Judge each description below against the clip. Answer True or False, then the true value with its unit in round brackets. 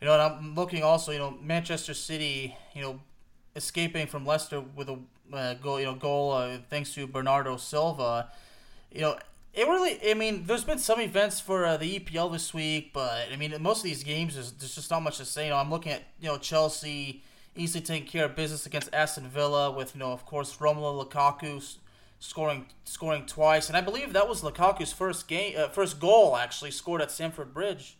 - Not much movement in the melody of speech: False (3.2 semitones)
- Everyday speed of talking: False (215 wpm)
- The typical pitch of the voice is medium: True (150 Hz)